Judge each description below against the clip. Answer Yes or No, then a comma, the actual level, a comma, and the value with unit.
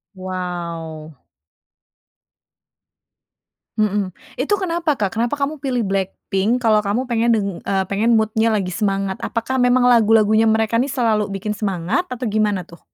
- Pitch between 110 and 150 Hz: No, high, 215 Hz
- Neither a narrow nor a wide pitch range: Yes, average, 3.5 semitones